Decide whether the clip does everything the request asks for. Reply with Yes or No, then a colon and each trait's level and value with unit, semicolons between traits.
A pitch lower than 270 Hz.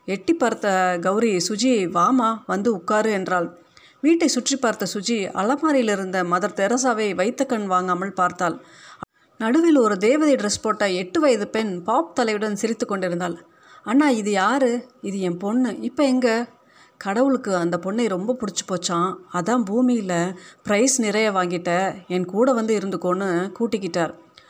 Yes: high, 215 Hz